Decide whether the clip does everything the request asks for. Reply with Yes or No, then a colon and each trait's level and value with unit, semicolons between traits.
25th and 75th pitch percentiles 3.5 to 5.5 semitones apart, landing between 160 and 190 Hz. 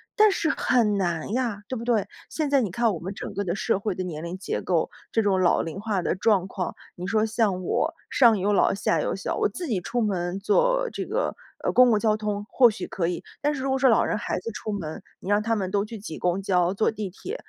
No: average, 3.9 semitones; high, 205 Hz